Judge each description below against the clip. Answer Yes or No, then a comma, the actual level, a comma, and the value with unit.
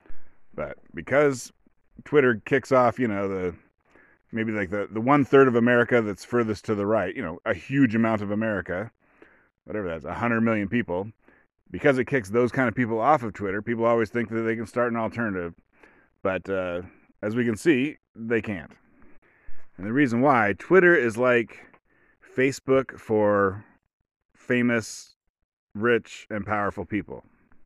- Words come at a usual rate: Yes, average, 160 wpm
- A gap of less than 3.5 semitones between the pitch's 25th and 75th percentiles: Yes, average, 3.0 semitones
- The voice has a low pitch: Yes, low, 115 Hz